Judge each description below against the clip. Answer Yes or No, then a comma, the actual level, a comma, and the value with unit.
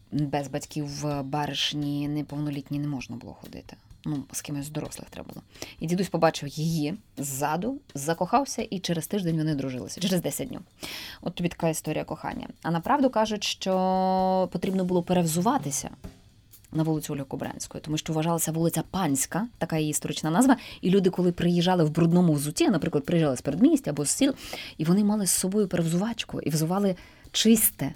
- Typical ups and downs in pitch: Yes, average, 4.3 semitones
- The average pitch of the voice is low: No, medium, 165 Hz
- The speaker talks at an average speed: No, fast, 165 wpm